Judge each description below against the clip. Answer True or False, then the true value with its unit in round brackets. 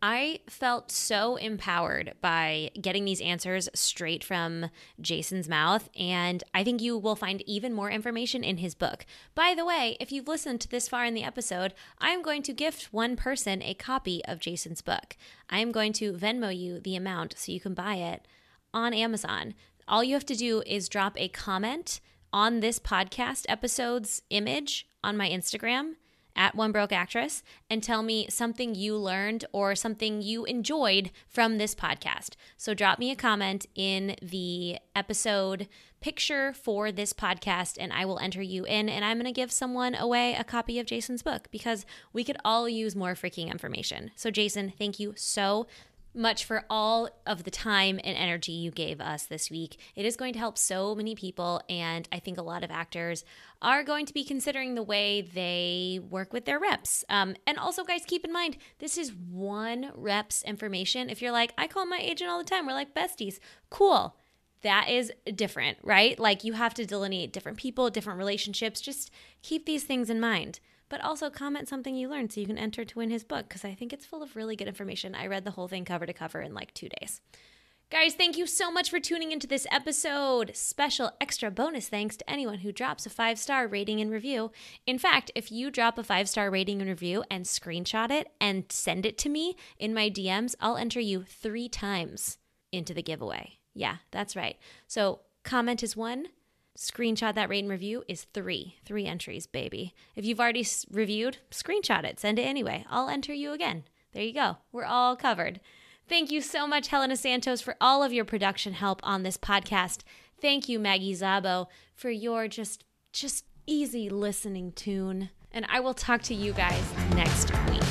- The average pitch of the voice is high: True (220 Hz)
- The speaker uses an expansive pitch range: False (4.4 semitones)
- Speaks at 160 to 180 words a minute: False (195 wpm)